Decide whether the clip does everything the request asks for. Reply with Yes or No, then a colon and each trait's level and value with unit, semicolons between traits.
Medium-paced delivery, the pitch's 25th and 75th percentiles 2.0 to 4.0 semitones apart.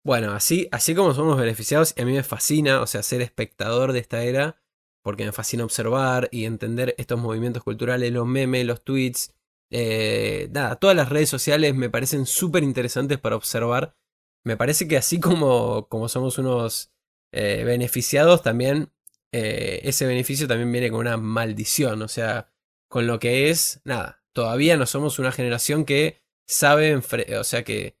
Yes: average, 170 wpm; average, 3.7 semitones